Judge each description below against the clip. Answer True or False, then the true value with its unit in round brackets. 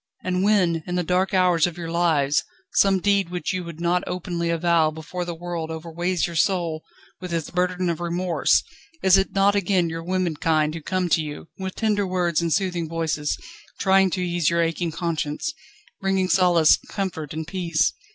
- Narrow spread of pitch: True (2.1 semitones)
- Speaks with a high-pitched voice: False (175 Hz)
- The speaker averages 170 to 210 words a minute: True (180 wpm)